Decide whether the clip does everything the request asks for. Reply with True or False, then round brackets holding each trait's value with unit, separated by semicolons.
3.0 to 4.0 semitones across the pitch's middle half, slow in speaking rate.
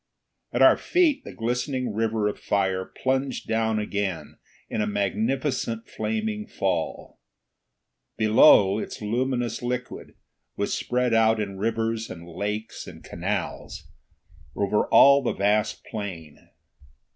True (3.5 semitones; 120 wpm)